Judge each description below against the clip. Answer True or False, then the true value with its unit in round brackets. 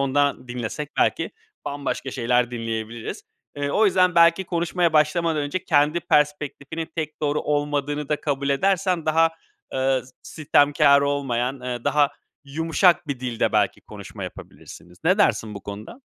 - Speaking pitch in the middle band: True (145 Hz)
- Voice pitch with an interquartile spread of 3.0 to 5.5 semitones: True (3.8 semitones)